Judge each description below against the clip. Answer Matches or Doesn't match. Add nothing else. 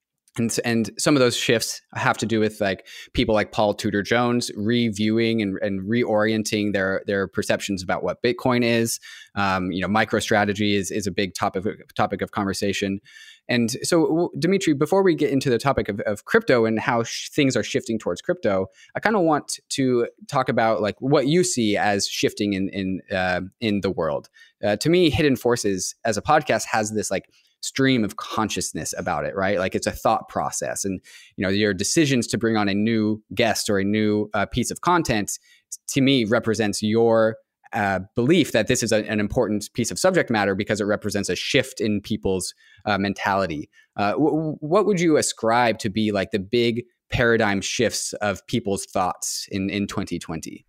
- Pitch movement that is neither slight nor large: Matches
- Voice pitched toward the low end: Matches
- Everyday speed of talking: Matches